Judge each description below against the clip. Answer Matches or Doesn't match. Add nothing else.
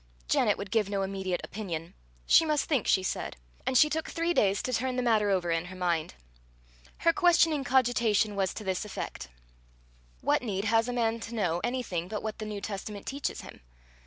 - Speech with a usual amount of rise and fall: Matches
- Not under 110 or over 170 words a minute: Doesn't match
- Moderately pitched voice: Doesn't match